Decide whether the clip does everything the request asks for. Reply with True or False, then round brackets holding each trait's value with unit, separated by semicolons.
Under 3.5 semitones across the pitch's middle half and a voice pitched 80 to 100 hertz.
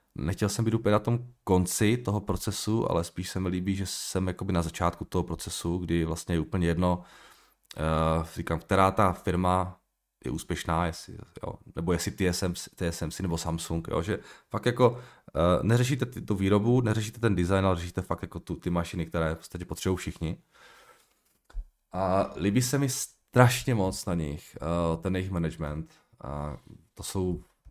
False (3.8 semitones; 90 Hz)